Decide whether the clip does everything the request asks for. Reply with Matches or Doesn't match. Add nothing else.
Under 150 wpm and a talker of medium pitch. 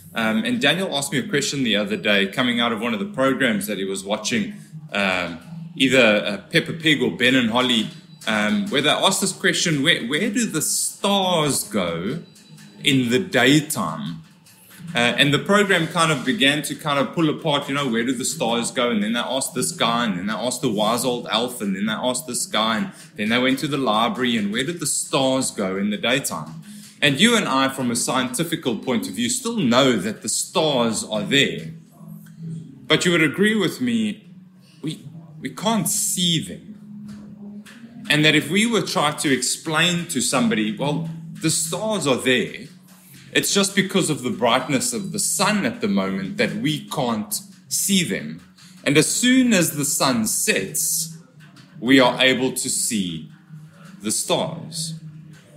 Doesn't match